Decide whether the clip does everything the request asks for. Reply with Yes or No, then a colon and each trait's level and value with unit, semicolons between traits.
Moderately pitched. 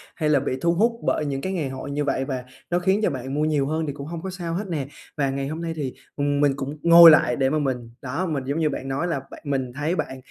Yes: medium, 145 Hz